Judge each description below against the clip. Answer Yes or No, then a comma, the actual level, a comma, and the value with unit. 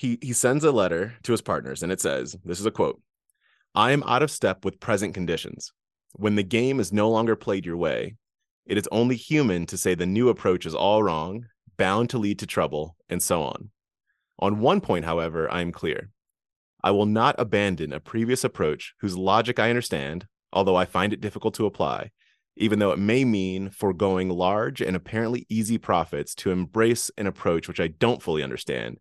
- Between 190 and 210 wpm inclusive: Yes, average, 200 wpm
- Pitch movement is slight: No, average, 3.7 semitones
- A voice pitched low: Yes, low, 105 Hz